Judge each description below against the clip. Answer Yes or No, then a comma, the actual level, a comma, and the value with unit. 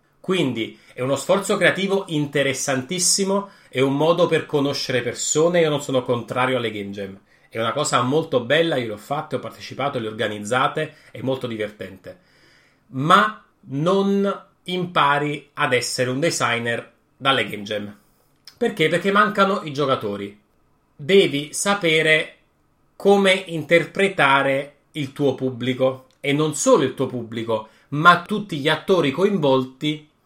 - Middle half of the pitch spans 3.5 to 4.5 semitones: No, average, 5.2 semitones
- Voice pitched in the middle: Yes, medium, 145 Hz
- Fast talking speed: No, average, 135 wpm